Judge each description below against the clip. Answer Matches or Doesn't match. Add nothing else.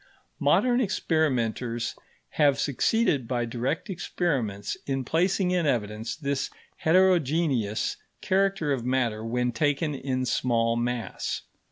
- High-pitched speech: Doesn't match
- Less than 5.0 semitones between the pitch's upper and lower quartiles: Doesn't match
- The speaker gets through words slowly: Matches